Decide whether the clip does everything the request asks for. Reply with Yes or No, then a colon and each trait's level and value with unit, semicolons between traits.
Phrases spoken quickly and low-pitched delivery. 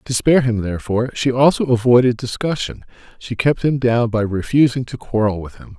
No: average, 185 wpm; low, 120 Hz